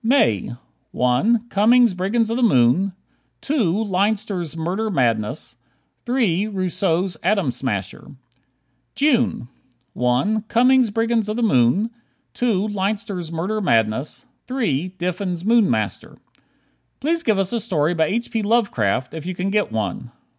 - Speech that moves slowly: Yes, slow, 130 wpm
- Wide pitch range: Yes, wide, 5.7 semitones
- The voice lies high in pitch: Yes, high, 195 Hz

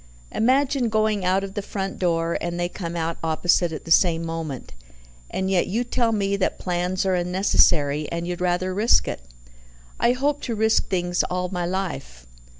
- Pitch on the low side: No, medium, 180 Hz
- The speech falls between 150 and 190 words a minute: Yes, average, 180 wpm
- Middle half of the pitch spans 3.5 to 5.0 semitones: No, average, 3.1 semitones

